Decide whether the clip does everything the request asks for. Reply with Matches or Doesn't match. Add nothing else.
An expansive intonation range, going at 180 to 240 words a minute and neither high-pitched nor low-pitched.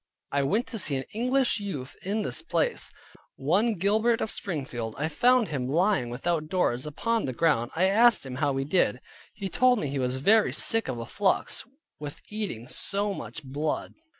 Matches